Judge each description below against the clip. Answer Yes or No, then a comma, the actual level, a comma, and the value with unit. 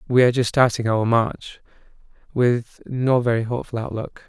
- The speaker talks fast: No, average, 155 wpm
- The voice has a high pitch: No, low, 120 Hz